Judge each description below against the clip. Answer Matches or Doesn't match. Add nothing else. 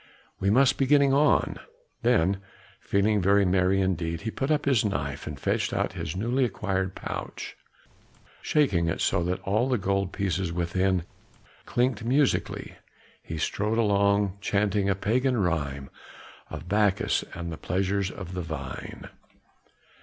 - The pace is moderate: Matches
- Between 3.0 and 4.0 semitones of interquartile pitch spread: Matches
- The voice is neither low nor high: Doesn't match